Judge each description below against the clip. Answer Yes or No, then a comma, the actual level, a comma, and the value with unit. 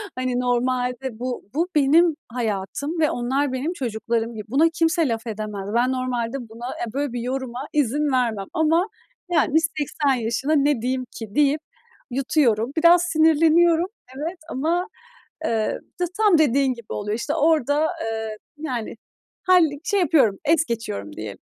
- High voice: Yes, very high, 260 Hz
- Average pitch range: Yes, average, 5.0 semitones